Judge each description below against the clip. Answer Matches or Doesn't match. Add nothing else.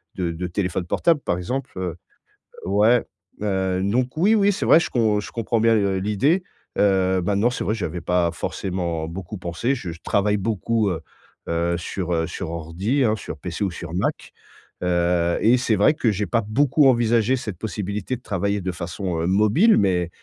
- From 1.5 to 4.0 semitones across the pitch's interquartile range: Doesn't match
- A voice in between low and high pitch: Doesn't match